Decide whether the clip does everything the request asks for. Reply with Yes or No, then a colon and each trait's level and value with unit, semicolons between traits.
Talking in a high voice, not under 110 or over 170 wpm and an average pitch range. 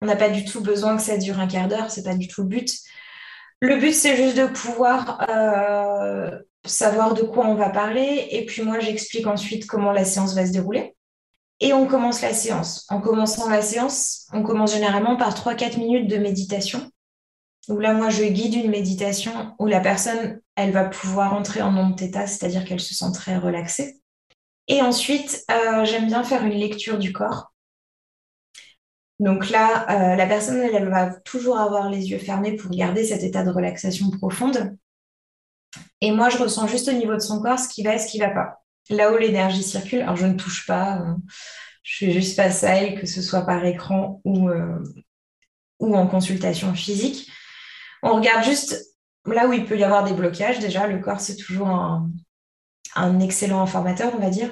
No: high, 210 Hz; average, 200 wpm; average, 3.1 semitones